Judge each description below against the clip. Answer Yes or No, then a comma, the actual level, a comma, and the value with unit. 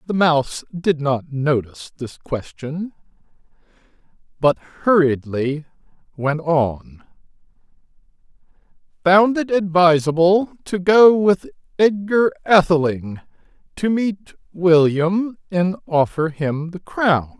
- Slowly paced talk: Yes, slow, 95 wpm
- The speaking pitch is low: No, medium, 170 Hz